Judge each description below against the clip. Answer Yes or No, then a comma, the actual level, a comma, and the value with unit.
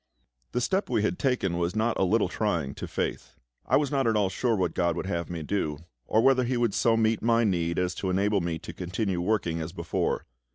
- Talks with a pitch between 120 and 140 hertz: No, low, 100 Hz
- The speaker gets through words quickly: Yes, fast, 235 wpm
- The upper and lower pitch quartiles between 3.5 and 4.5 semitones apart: No, average, 4.9 semitones